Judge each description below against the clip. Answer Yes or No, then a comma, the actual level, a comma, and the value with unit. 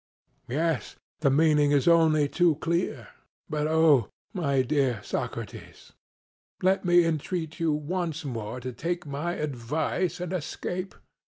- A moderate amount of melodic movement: Yes, average, 3.2 semitones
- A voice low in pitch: No, medium, 155 Hz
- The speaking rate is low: Yes, slow, 130 wpm